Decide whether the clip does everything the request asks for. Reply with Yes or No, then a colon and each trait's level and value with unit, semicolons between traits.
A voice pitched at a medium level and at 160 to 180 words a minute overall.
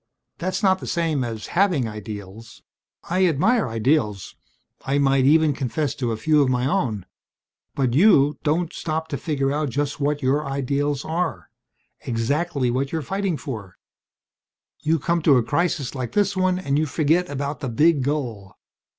Yes: medium, 145 Hz; average, 165 wpm